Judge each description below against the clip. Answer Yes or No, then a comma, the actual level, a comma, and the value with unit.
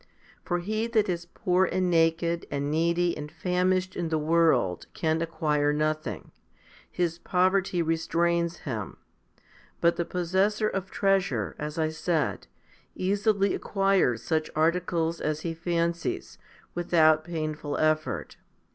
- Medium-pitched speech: Yes, medium, 170 Hz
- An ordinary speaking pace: No, slow, 125 wpm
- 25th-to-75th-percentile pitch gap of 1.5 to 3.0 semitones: Yes, narrow, 2.5 semitones